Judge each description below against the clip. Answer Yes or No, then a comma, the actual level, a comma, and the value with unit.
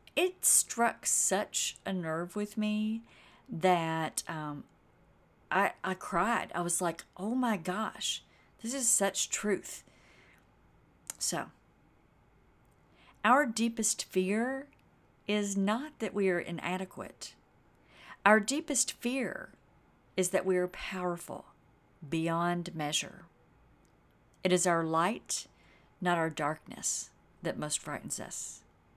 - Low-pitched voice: No, high, 190 Hz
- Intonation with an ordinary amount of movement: Yes, average, 4.3 semitones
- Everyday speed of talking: No, slow, 110 wpm